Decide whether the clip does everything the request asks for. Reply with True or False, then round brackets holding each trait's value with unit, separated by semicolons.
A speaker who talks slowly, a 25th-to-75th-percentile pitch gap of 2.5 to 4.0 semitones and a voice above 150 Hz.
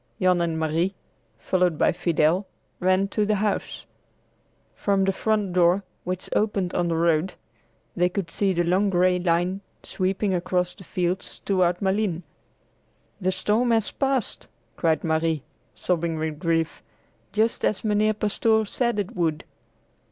False (145 wpm; 2.9 semitones; 185 Hz)